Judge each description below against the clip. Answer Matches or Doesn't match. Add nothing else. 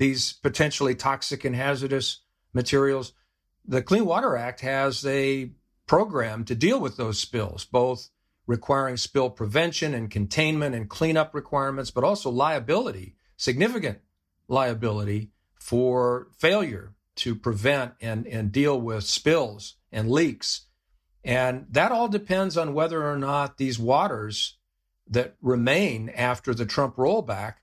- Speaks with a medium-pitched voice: Doesn't match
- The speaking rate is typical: Doesn't match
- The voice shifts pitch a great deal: Doesn't match